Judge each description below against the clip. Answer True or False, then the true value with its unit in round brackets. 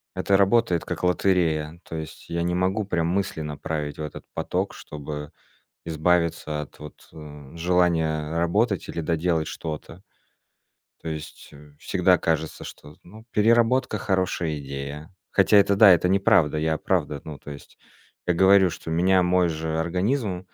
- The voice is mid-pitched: False (85 Hz)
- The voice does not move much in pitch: False (3.4 semitones)